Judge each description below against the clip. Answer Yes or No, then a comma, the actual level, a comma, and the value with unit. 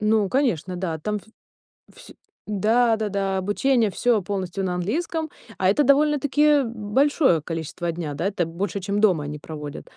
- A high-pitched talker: Yes, high, 205 Hz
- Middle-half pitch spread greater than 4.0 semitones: Yes, wide, 5.5 semitones